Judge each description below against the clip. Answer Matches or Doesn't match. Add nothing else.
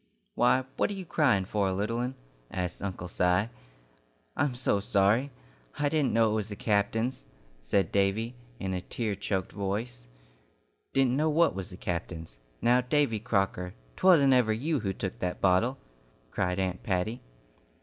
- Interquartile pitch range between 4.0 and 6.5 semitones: Matches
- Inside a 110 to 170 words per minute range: Matches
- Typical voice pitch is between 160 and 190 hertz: Doesn't match